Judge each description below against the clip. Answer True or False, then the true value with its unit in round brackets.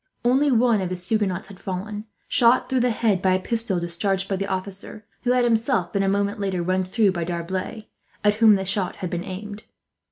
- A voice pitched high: True (200 Hz)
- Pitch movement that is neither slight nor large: True (3.1 semitones)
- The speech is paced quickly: True (215 wpm)